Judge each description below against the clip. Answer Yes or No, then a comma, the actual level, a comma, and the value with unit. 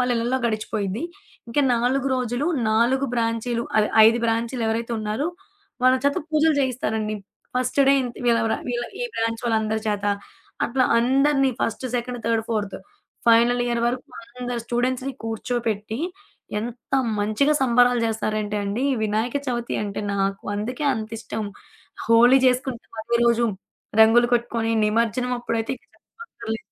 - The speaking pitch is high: Yes, high, 235 Hz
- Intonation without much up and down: Yes, narrow, 2.1 semitones